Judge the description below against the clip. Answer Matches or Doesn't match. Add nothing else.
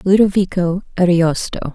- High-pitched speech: Doesn't match